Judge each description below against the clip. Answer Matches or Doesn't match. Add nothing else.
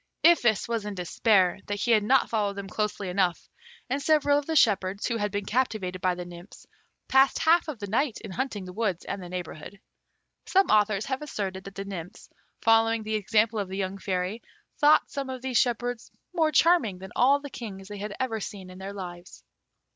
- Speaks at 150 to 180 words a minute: Doesn't match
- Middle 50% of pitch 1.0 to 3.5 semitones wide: Doesn't match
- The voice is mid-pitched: Doesn't match